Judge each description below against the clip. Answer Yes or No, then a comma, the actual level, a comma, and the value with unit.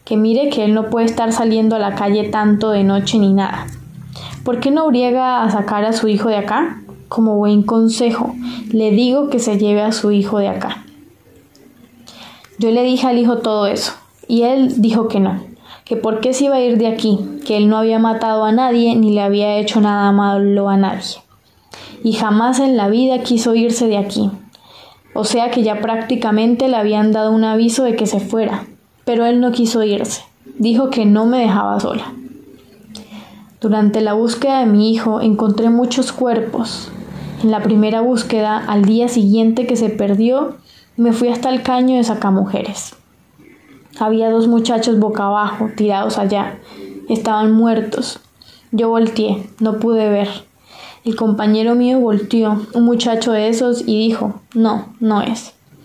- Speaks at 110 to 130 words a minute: No, average, 175 wpm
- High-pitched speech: Yes, high, 220 Hz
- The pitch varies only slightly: Yes, narrow, 2.1 semitones